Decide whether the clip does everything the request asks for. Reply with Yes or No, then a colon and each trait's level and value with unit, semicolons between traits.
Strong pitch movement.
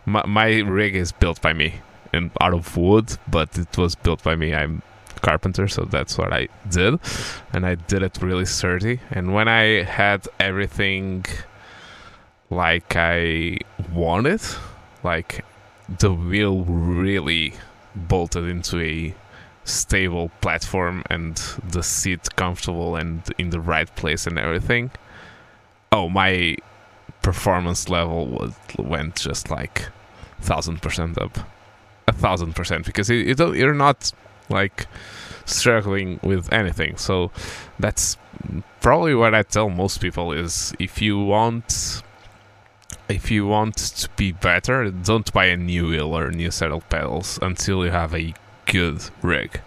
No: average, 3.9 semitones